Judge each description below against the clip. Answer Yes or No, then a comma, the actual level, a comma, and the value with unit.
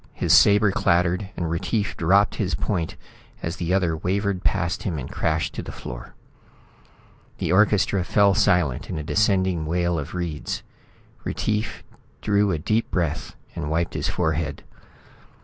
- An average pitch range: Yes, average, 3.5 semitones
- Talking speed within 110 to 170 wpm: Yes, average, 150 wpm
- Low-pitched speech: Yes, very low, 90 Hz